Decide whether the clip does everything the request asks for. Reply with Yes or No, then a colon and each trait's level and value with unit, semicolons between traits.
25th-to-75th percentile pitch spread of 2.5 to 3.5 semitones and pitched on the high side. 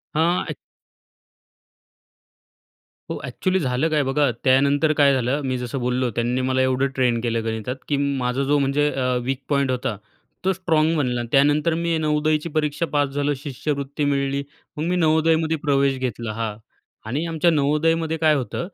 No: average, 3.1 semitones; medium, 140 Hz